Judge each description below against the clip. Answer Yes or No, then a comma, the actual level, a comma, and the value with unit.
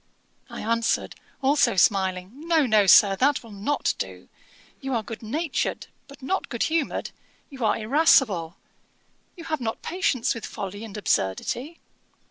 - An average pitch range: No, wide, 6.0 semitones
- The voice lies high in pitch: Yes, high, 230 Hz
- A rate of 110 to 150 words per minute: Yes, average, 145 wpm